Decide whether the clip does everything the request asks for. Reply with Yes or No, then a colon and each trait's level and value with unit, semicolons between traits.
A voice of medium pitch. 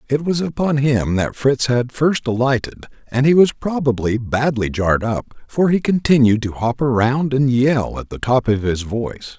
No: low, 130 Hz